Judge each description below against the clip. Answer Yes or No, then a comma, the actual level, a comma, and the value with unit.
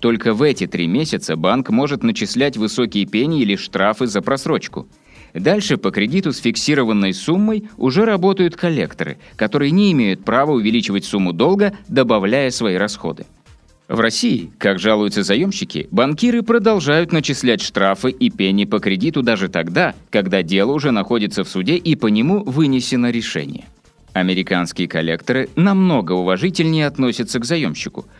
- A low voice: Yes, low, 130 Hz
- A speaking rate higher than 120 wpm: Yes, average, 140 wpm